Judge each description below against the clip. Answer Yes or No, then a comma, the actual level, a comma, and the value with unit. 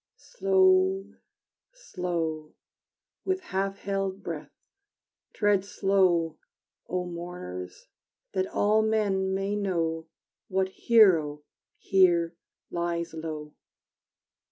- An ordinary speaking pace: No, slow, 85 wpm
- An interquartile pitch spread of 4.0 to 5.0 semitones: No, average, 3.5 semitones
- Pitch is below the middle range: No, high, 190 Hz